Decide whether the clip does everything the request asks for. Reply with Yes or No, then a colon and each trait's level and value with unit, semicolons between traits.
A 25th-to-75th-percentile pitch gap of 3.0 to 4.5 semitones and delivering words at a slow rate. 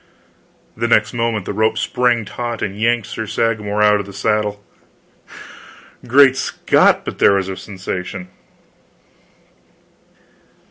No: narrow, 2.6 semitones; slow, 125 wpm